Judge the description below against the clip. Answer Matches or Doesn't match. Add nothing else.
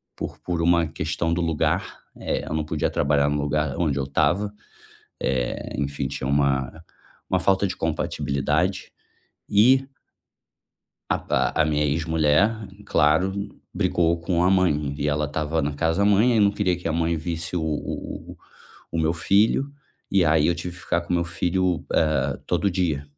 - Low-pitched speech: Matches